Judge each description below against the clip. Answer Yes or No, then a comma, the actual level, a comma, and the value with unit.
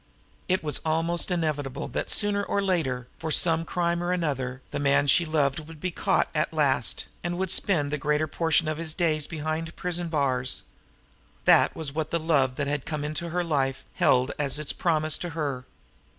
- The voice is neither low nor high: Yes, medium, 155 Hz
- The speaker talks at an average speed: Yes, average, 190 wpm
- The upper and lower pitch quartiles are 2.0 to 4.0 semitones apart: Yes, average, 3.0 semitones